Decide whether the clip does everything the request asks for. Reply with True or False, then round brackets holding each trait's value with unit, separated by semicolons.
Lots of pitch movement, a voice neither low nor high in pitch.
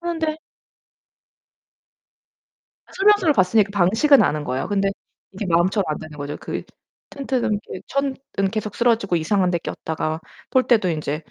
False (7.7 semitones; 200 Hz)